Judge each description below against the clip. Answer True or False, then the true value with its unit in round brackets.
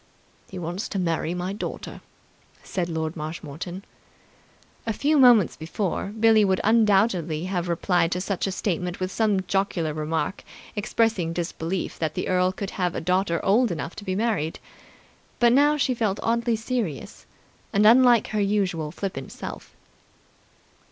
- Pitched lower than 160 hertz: False (190 Hz)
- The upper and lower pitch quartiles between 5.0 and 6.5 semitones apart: False (4.1 semitones)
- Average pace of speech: True (150 wpm)